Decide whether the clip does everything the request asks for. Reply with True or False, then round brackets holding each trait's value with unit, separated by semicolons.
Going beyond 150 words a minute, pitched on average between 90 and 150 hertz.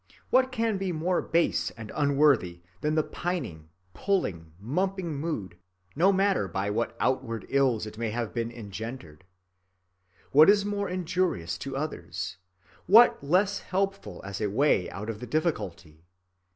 False (145 wpm; 140 Hz)